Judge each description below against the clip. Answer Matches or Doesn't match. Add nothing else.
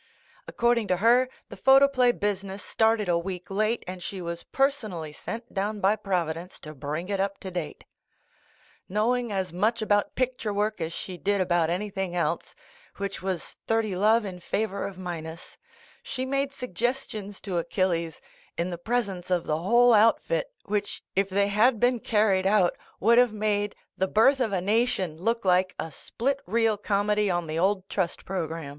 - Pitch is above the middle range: Matches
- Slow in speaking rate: Doesn't match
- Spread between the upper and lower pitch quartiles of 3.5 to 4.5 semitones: Matches